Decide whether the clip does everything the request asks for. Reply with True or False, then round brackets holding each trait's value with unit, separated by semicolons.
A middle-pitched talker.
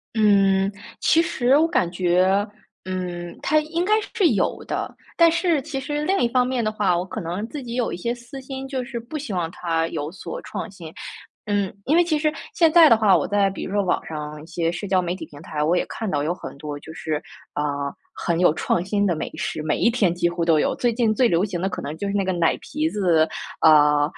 False (195 Hz)